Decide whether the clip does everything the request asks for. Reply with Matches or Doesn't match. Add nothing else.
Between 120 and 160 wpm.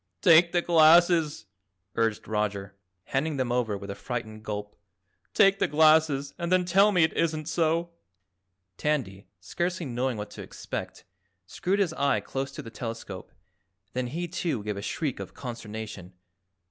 Matches